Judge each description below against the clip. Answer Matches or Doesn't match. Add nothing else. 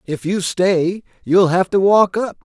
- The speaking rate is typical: Matches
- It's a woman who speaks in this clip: Doesn't match